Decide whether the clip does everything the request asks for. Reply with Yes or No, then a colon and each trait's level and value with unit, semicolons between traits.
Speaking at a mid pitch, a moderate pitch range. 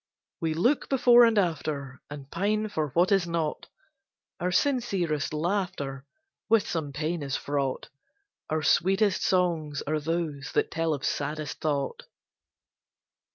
Yes: medium, 160 Hz; average, 4.5 semitones